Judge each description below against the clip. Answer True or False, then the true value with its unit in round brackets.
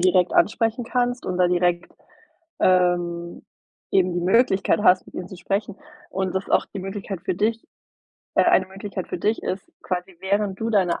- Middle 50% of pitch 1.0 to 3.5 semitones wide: True (2.5 semitones)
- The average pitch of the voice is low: False (190 Hz)